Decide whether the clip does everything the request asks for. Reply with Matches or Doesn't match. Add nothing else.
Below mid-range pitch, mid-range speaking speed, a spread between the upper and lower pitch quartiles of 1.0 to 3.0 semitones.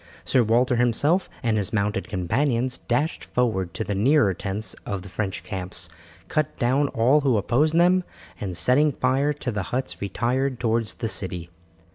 Doesn't match